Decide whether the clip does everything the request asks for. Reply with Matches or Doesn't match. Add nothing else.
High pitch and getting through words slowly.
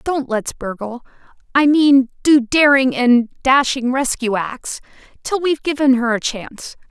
Matches